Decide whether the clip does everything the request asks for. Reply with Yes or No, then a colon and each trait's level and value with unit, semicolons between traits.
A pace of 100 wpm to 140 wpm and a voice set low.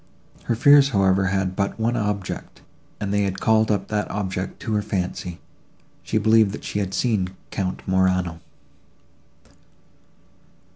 Yes: slow, 135 wpm; low, 100 Hz